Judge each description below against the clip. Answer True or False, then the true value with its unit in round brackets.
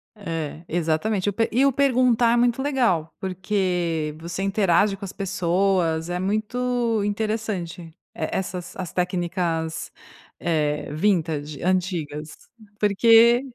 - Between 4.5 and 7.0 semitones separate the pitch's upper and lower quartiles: True (4.8 semitones)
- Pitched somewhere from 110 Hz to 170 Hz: False (185 Hz)